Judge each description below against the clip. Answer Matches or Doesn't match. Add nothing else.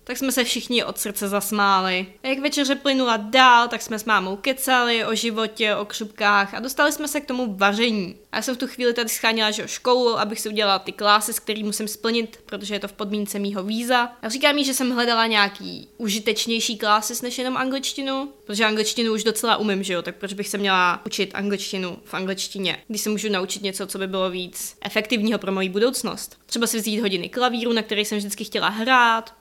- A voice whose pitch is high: Matches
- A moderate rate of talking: Doesn't match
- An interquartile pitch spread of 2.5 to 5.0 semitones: Matches